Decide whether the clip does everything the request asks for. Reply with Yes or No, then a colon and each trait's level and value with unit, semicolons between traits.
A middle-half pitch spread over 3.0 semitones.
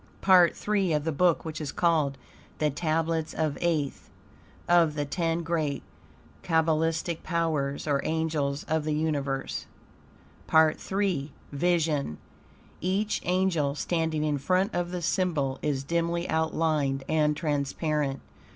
No: narrow, 2.6 semitones